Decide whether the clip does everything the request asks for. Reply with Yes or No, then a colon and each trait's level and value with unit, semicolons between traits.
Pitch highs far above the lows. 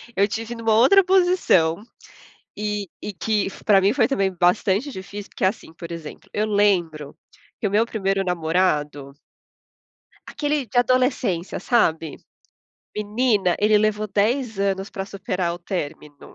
No: average, 3.9 semitones